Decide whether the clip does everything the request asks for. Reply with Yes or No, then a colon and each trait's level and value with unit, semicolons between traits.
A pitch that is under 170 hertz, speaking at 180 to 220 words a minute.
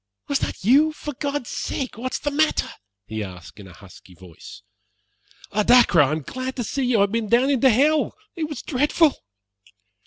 No: very high, 250 Hz; average, 190 wpm